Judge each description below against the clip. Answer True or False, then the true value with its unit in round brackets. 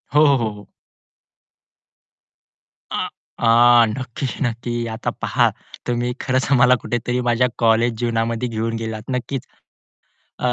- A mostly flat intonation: True (1.7 semitones)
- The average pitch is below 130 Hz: True (120 Hz)